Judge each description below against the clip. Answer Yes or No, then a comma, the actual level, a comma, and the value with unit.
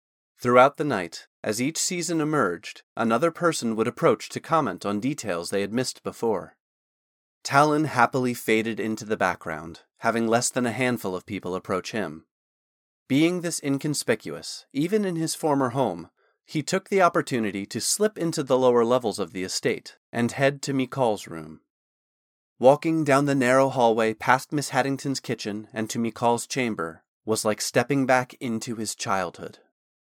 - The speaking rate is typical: Yes, average, 160 wpm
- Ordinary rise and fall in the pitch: Yes, average, 4.3 semitones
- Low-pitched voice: Yes, low, 125 Hz